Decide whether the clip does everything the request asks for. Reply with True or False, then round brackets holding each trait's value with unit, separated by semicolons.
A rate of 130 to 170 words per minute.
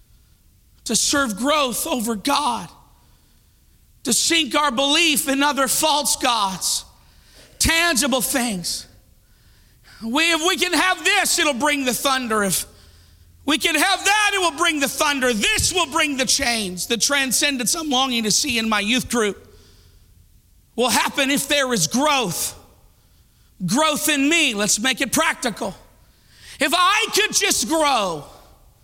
True (140 wpm)